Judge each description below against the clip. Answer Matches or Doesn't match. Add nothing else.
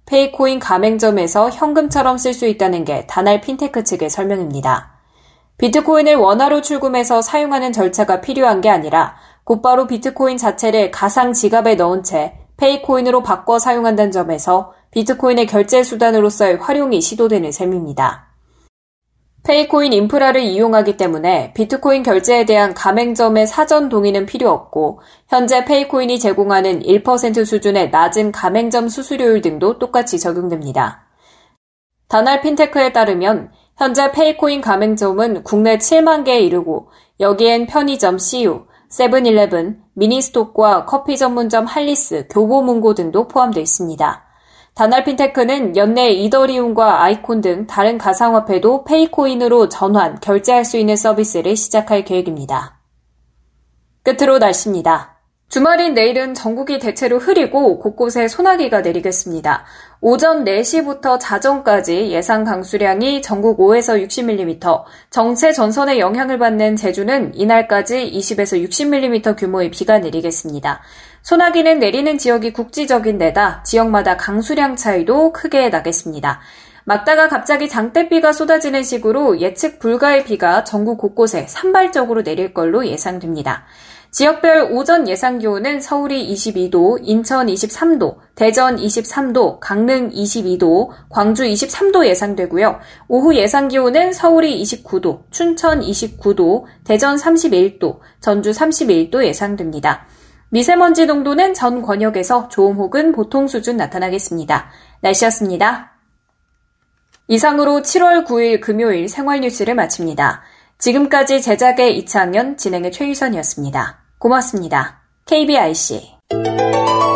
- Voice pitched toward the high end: Matches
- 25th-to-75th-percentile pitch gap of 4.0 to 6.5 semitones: Matches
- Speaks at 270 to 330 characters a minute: Matches